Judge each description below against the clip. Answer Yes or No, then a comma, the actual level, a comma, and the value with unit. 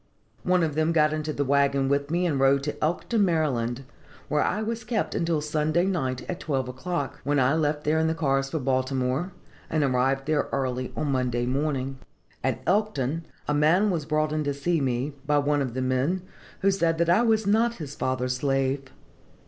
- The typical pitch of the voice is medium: Yes, medium, 150 Hz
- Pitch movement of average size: Yes, average, 3.7 semitones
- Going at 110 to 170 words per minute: No, average, 195 wpm